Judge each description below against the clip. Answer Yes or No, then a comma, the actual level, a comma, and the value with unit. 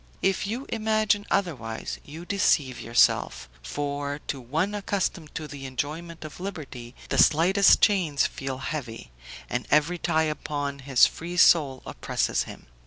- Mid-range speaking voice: Yes, medium, 155 Hz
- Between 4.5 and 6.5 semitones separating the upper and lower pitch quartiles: Yes, average, 5.2 semitones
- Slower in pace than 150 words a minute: Yes, average, 140 wpm